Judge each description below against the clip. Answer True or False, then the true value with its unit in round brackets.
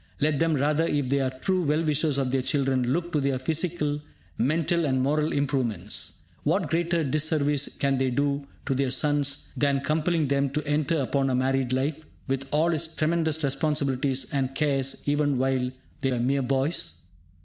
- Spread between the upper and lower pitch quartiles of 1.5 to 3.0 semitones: True (2.5 semitones)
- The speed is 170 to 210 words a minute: True (175 wpm)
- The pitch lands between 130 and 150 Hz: True (140 Hz)